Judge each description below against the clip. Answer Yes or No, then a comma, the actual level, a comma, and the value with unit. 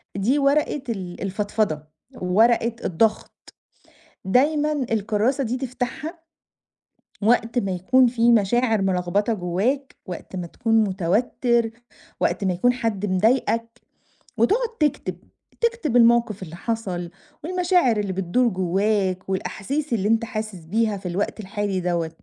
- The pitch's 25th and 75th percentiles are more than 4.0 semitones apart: Yes, average, 4.5 semitones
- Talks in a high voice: Yes, high, 220 Hz